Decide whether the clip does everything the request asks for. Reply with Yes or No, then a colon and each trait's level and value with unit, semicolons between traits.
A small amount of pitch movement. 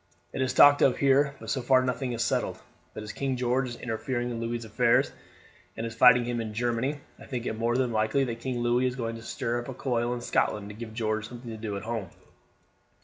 Yes: narrow, 1.9 semitones